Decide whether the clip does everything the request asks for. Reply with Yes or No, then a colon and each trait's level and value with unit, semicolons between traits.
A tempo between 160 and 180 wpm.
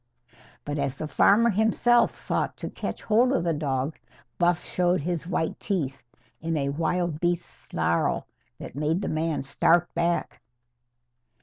No: average, 145 wpm